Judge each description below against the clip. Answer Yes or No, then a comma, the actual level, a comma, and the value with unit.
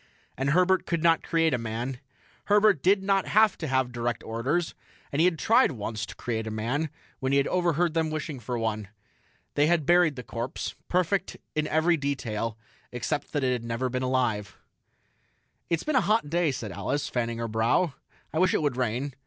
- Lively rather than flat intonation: Yes, wide, 6.2 semitones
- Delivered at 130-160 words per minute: No, average, 195 wpm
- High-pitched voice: No, medium, 140 Hz